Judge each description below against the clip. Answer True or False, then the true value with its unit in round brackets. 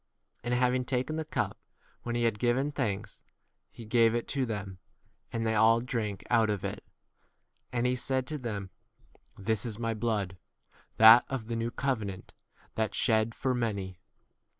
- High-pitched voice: False (115 Hz)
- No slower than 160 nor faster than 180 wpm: True (175 wpm)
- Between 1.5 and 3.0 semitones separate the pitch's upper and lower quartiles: True (2.7 semitones)